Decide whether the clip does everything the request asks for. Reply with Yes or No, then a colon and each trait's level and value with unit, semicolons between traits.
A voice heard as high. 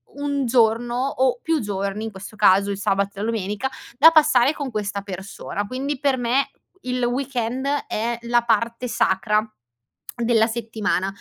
Yes: high, 235 Hz